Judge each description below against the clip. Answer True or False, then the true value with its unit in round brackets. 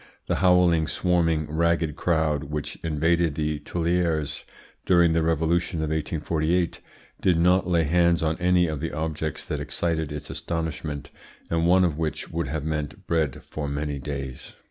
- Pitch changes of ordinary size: False (2.0 semitones)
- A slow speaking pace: False (155 wpm)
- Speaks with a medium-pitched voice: False (80 Hz)